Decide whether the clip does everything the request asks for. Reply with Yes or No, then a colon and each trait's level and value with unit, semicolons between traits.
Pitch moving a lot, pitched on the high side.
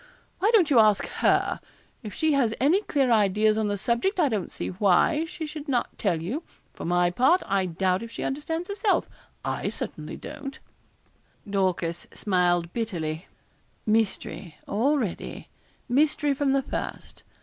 Yes: wide, 7.5 semitones; high, 225 Hz